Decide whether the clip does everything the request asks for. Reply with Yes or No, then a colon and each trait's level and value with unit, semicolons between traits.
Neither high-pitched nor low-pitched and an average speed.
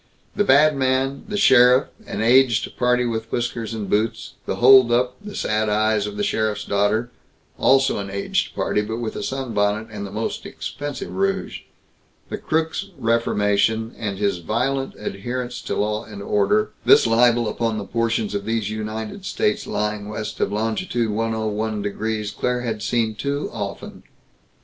No: low, 115 Hz; average, 155 wpm